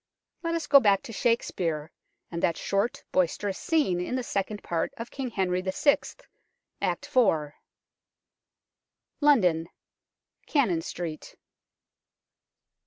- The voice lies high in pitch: Yes, high, 195 Hz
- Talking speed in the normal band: No, slow, 110 wpm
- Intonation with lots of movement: Yes, wide, 6.6 semitones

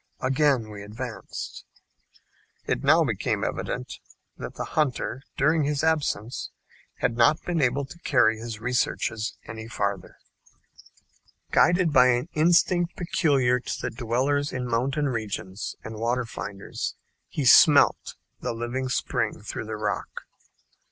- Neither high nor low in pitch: No, low, 125 Hz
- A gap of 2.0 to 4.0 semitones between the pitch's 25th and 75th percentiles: No, average, 4.5 semitones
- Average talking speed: No, slow, 130 wpm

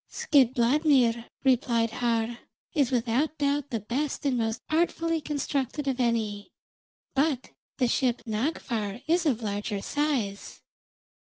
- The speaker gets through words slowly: Yes, slow, 115 wpm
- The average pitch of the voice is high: Yes, very high, 250 Hz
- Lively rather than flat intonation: No, average, 4.0 semitones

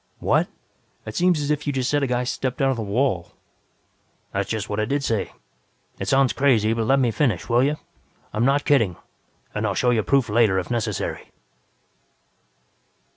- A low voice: Yes, low, 120 Hz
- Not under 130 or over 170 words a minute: No, average, 185 wpm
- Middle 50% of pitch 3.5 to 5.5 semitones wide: Yes, average, 4.2 semitones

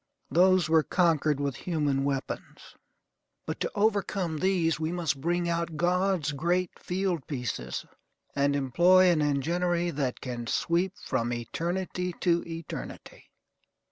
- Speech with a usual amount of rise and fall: Yes, average, 4.1 semitones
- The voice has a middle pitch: Yes, medium, 170 Hz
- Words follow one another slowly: Yes, slow, 120 wpm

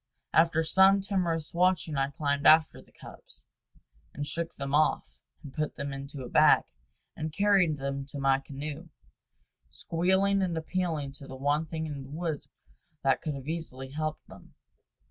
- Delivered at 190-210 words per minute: No, average, 165 wpm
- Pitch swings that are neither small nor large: Yes, average, 3.3 semitones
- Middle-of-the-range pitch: Yes, medium, 155 Hz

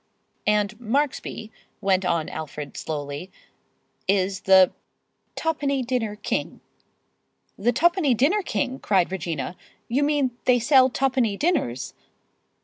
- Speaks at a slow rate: Yes, slow, 110 wpm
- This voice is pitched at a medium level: No, high, 225 Hz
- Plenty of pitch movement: Yes, wide, 6.4 semitones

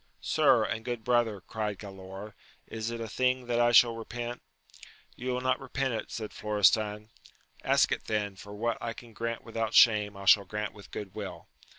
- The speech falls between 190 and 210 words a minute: Yes, average, 195 wpm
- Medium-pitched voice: No, low, 110 Hz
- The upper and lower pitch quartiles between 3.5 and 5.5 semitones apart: No, narrow, 2.4 semitones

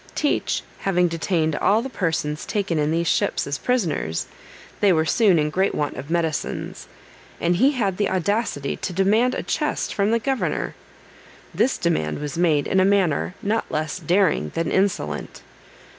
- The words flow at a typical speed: Yes, average, 165 wpm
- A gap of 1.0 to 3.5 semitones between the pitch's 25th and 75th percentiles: No, average, 4.6 semitones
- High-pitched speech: No, medium, 180 Hz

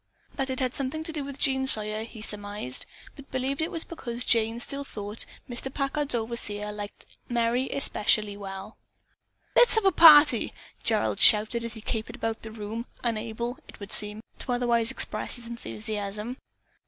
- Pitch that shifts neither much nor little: Yes, average, 3.7 semitones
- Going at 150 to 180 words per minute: Yes, average, 170 wpm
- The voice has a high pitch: Yes, high, 235 Hz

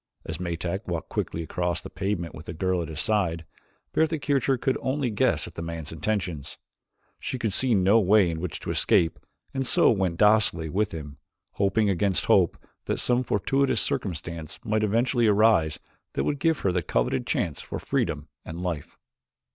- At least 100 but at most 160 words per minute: No, average, 180 wpm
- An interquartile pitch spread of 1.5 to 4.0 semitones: No, average, 4.9 semitones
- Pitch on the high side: No, very low, 95 Hz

